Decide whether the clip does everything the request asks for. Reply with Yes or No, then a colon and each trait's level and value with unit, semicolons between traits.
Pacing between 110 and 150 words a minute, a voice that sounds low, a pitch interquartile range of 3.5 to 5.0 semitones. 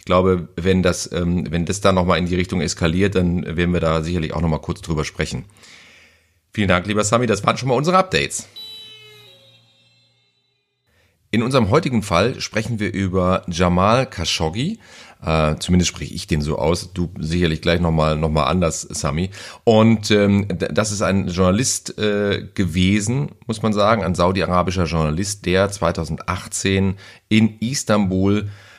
Yes: average, 145 wpm; very low, 95 Hz; average, 3.9 semitones